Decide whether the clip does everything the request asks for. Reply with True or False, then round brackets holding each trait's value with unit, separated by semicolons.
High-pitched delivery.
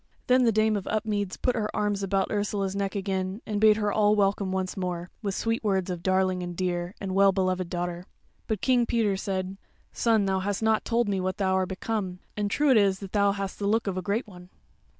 True (195 Hz)